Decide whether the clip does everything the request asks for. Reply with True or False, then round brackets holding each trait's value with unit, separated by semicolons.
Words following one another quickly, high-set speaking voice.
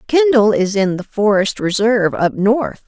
False (165 wpm; 215 Hz)